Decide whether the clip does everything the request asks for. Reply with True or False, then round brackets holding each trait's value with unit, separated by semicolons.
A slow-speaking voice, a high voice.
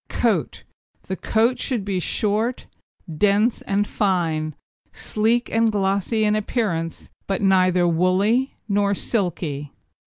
True (120 wpm; 200 Hz)